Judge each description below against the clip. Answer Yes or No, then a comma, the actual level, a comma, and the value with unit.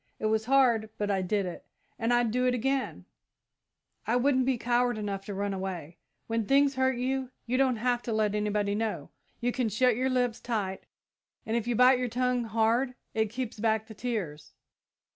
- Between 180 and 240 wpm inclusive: Yes, average, 195 wpm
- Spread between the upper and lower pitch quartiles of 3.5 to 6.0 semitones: No, average, 3.0 semitones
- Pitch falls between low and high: No, high, 230 Hz